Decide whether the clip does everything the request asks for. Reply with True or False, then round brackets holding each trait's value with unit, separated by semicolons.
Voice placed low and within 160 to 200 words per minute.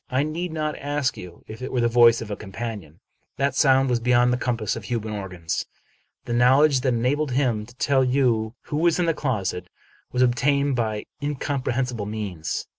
True (125 Hz; 190 wpm)